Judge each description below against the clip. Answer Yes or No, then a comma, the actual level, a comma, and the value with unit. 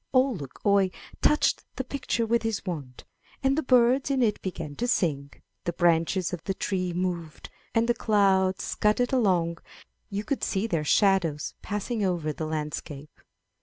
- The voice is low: No, high, 190 Hz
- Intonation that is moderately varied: No, wide, 5.7 semitones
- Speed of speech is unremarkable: Yes, average, 165 wpm